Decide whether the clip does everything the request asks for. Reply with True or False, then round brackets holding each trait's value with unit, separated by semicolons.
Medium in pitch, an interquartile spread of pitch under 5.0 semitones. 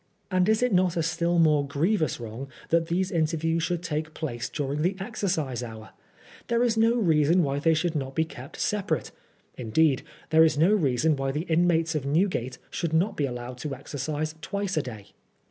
True (160 Hz; 3.9 semitones)